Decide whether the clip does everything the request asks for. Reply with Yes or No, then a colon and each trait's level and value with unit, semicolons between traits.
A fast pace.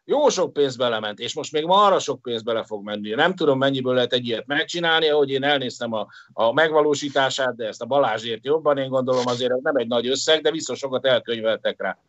Yes: fast, 225 wpm